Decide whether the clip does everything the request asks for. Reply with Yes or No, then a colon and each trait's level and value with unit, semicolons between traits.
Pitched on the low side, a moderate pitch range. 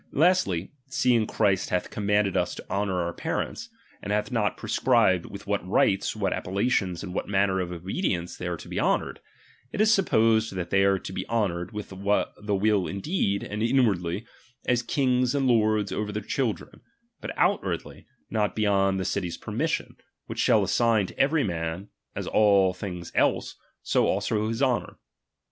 Yes: low, 105 Hz; average, 3.3 semitones